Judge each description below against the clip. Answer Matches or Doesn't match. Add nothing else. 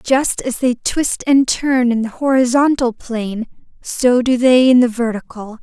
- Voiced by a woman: Matches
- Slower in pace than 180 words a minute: Matches